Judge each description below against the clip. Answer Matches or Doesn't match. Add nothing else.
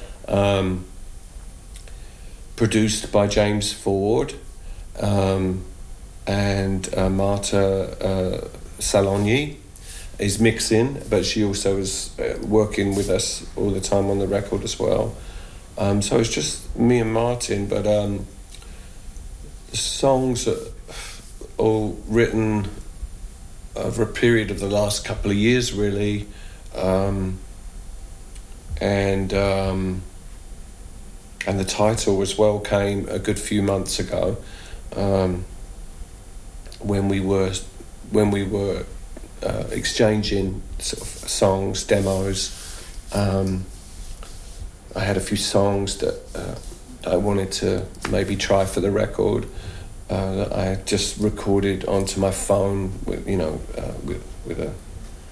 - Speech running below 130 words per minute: Matches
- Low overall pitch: Matches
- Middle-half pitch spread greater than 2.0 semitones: Doesn't match